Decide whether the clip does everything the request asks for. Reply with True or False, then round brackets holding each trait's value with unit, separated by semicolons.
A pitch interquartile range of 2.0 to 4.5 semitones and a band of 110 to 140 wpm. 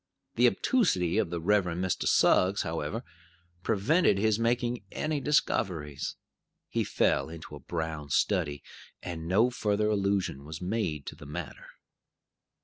False (5.4 semitones; 135 wpm)